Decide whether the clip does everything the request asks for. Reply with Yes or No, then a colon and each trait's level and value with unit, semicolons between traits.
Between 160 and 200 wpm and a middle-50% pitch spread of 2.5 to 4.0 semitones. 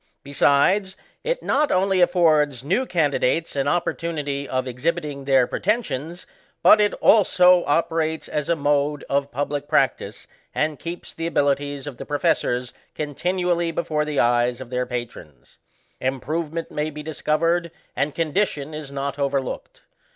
No: average, 145 wpm; average, 3.4 semitones